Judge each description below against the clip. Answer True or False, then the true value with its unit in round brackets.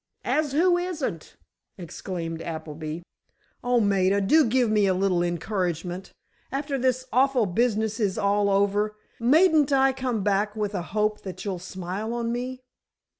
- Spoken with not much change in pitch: False (5.3 semitones)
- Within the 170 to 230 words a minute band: False (145 wpm)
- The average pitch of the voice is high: True (210 Hz)